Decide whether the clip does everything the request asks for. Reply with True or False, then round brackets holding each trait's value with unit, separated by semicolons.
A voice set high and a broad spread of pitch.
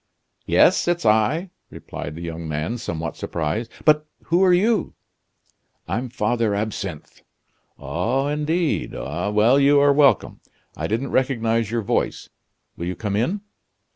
False (115 Hz; 6.1 semitones)